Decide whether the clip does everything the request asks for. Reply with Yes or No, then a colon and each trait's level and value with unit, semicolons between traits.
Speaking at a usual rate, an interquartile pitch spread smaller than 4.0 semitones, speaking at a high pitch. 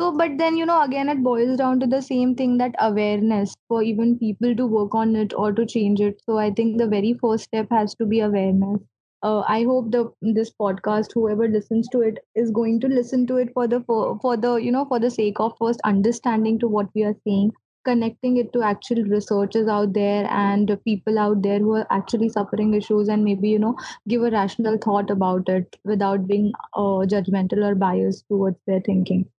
No: fast, 215 wpm; narrow, 2.4 semitones; high, 220 Hz